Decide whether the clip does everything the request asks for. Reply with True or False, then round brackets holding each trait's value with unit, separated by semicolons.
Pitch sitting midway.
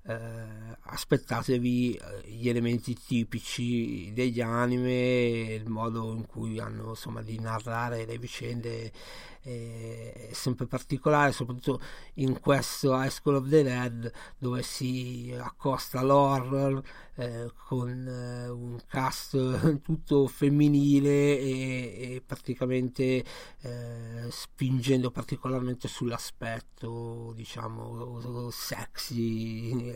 False (125 Hz)